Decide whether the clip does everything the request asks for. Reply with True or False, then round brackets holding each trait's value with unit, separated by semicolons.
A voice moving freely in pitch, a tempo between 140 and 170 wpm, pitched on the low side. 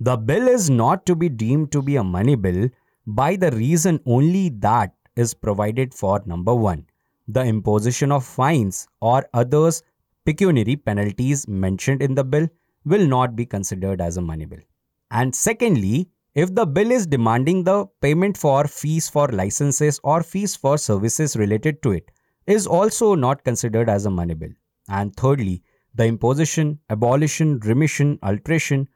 True (6.4 semitones; 160 wpm; 130 Hz)